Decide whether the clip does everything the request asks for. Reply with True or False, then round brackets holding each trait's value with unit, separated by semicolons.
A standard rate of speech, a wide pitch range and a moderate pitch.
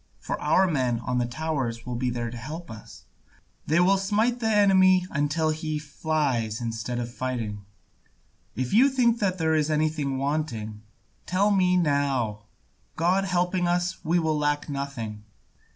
True (150 wpm; 6.6 semitones; 150 Hz)